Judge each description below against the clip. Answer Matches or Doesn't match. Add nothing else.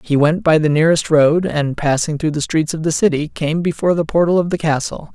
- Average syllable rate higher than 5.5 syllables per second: Matches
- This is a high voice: Doesn't match